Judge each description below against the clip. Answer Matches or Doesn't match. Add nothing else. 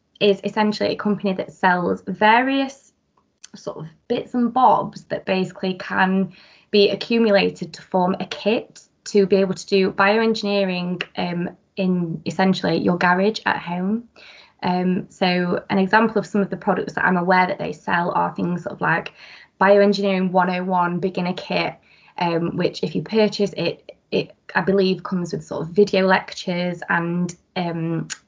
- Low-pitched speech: Doesn't match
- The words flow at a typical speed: Matches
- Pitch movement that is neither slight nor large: Doesn't match